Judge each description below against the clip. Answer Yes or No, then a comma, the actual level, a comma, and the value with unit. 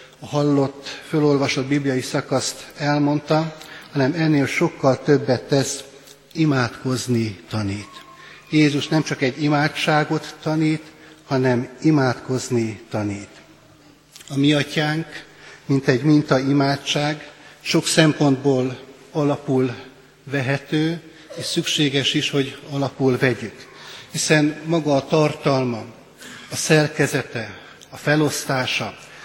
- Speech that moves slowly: Yes, slow, 95 wpm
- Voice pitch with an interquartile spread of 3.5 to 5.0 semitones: No, narrow, 2.6 semitones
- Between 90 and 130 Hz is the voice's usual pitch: No, medium, 140 Hz